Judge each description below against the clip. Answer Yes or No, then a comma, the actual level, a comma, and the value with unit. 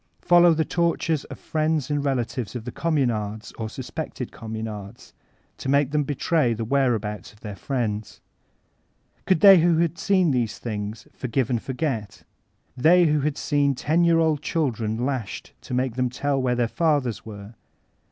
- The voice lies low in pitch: Yes, low, 130 Hz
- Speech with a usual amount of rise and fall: No, wide, 5.7 semitones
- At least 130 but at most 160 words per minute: No, average, 170 wpm